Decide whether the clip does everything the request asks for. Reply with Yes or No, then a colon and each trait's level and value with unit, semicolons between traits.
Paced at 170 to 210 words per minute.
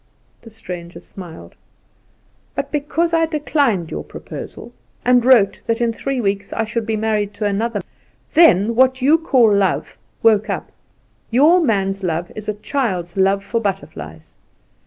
No: average, 150 wpm